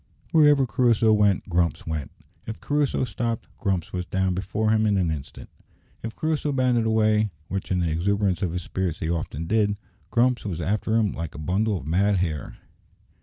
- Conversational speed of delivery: Yes, average, 180 wpm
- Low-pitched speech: Yes, low, 100 Hz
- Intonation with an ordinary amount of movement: Yes, average, 4.3 semitones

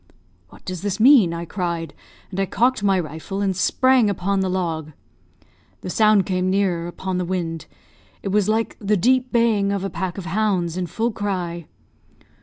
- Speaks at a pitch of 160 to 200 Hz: Yes, high, 190 Hz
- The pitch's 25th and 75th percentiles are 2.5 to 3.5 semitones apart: Yes, average, 3.0 semitones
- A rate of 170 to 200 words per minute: Yes, average, 180 wpm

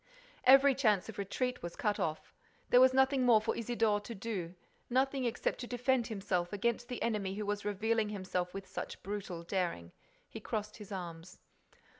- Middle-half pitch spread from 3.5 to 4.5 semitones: Yes, average, 4.1 semitones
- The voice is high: Yes, high, 210 Hz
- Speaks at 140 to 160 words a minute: No, average, 175 wpm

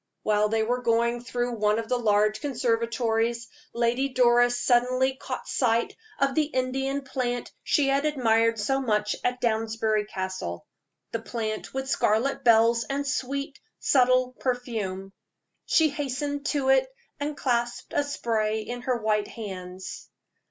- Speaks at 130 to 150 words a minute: Yes, average, 140 wpm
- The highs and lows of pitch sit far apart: No, average, 3.1 semitones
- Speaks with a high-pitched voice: Yes, high, 240 Hz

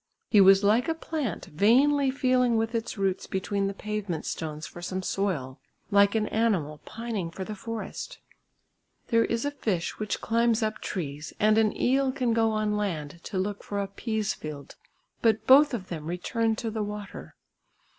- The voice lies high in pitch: Yes, high, 210 Hz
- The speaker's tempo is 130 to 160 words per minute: No, average, 175 wpm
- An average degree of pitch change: Yes, average, 3.4 semitones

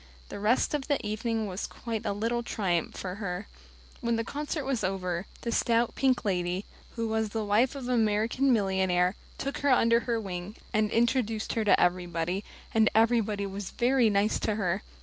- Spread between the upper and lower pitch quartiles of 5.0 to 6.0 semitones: No, average, 3.3 semitones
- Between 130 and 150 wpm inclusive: No, average, 185 wpm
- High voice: Yes, high, 220 Hz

